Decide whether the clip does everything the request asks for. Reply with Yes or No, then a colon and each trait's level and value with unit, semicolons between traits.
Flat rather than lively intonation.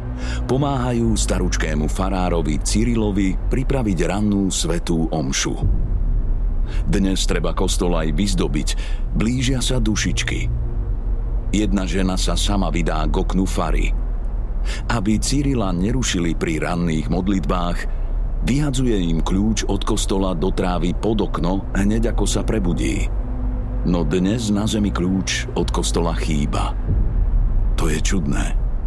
No: average, 4.2 semitones